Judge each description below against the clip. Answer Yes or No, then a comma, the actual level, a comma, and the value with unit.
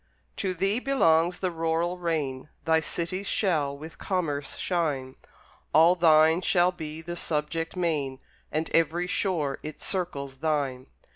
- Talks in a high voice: No, medium, 165 Hz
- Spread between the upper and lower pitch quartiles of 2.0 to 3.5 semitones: Yes, average, 2.9 semitones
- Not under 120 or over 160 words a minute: Yes, slow, 135 wpm